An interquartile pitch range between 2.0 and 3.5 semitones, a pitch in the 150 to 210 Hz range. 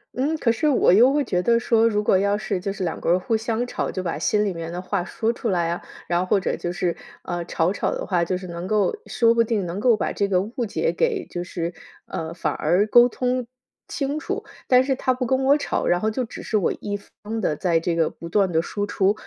No: average, 5.2 semitones; high, 205 Hz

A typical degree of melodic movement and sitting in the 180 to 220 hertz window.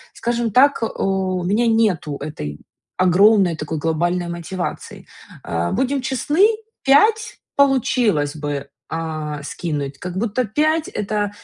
No: wide, 7.4 semitones; high, 190 Hz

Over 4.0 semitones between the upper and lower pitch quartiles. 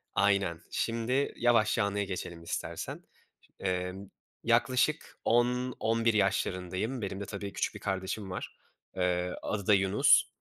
No: average, 3.7 semitones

